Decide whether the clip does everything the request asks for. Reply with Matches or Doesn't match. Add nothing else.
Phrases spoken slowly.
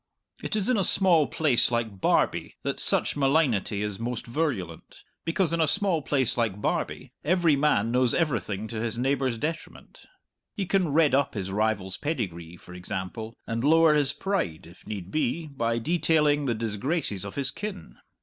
Doesn't match